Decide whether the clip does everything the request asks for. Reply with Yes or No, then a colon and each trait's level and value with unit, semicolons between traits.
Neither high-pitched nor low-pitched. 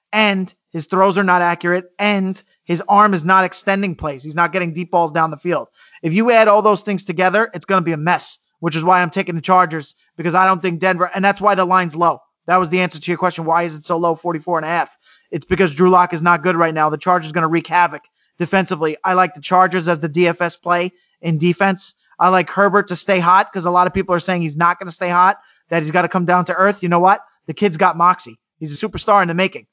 Yes: medium, 180 Hz